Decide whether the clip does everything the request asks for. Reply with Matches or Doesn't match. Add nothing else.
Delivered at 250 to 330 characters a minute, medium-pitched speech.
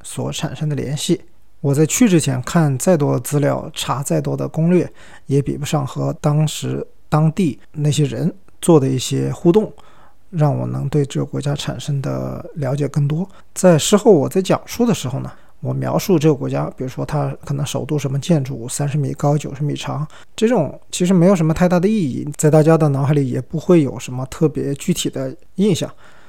Matches